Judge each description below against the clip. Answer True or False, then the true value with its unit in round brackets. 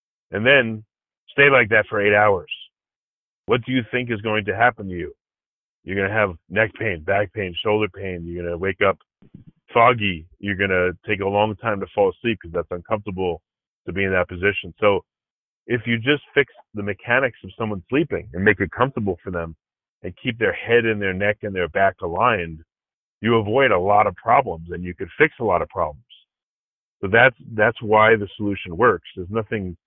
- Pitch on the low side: True (105 Hz)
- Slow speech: False (200 wpm)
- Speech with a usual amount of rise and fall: True (3.5 semitones)